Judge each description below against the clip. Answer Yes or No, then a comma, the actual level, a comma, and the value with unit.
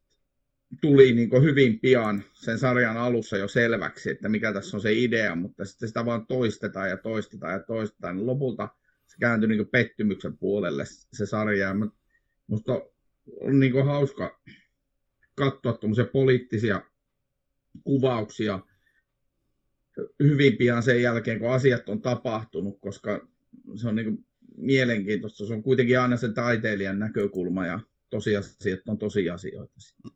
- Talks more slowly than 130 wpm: No, average, 135 wpm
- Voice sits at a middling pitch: No, low, 115 Hz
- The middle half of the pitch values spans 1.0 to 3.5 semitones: Yes, average, 3.1 semitones